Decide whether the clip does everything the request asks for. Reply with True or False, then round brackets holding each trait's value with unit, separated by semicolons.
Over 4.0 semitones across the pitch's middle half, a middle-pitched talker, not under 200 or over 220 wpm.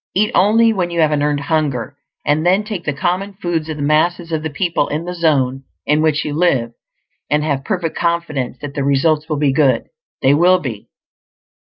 False (3.4 semitones; 155 Hz; 205 wpm)